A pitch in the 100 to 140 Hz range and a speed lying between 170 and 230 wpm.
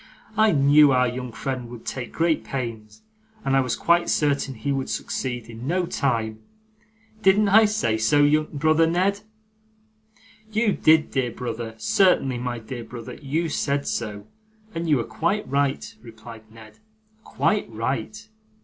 No: low, 135 Hz; average, 150 wpm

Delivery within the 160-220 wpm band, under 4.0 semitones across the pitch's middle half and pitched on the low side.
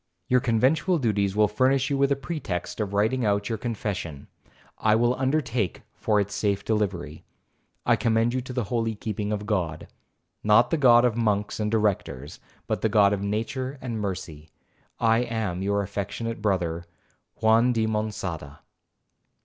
No: average, 150 wpm; average, 3.1 semitones; low, 110 Hz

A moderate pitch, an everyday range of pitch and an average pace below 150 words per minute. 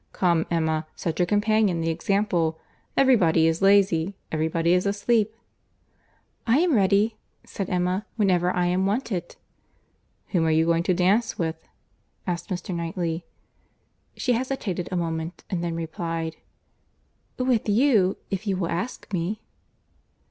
Yes: medium, 180 Hz; average, 3.8 semitones; average, 140 wpm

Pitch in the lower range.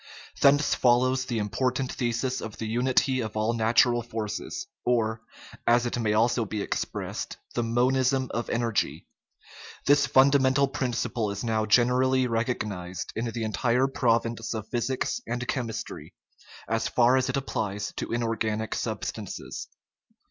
Yes: low, 120 Hz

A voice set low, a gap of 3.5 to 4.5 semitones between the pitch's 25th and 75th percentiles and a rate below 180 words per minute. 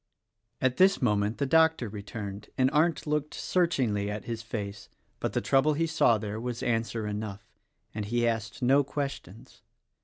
No: low, 115 Hz; average, 5.2 semitones; average, 160 wpm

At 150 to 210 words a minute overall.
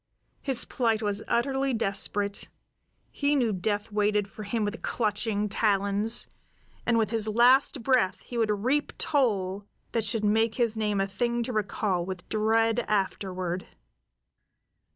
No: average, 140 wpm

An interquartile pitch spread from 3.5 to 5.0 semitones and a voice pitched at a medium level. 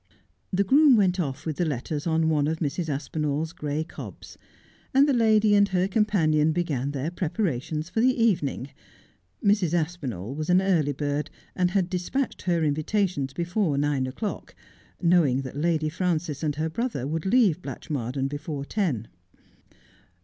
Yes: average, 4.5 semitones; medium, 160 Hz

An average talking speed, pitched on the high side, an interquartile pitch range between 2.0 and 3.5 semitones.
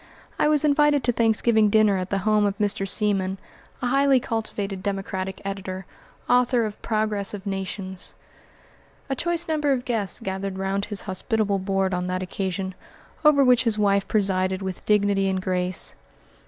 Yes: average, 160 wpm; high, 200 Hz; average, 3.2 semitones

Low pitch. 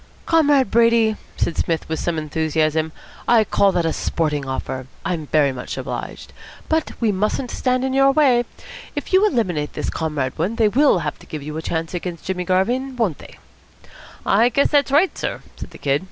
No: high, 190 Hz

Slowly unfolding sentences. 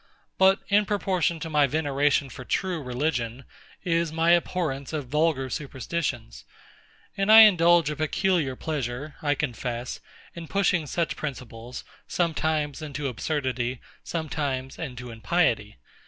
Yes: slow, 125 wpm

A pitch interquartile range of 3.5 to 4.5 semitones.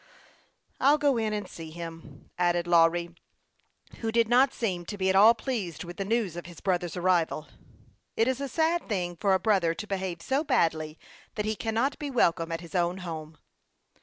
No: average, 4.9 semitones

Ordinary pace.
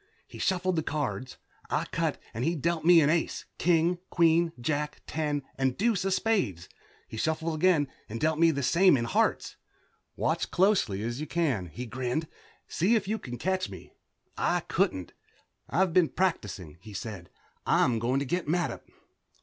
Yes: average, 175 wpm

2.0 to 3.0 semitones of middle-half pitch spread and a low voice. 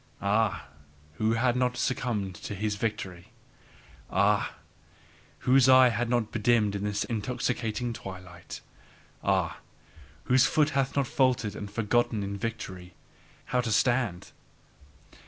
No: average, 3.5 semitones; low, 115 Hz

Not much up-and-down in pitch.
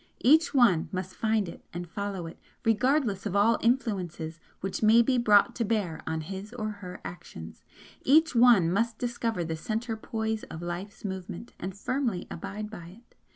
No: average, 4.5 semitones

